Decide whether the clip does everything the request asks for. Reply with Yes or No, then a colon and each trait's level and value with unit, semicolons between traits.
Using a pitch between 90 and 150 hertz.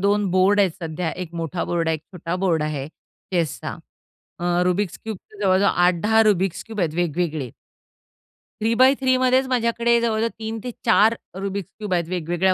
No: high, 190 Hz